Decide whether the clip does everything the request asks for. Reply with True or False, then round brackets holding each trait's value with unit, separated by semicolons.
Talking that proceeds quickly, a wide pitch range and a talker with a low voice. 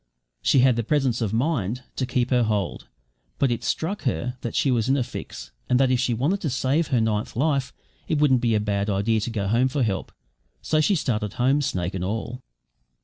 False (220 wpm; 3.6 semitones; 125 Hz)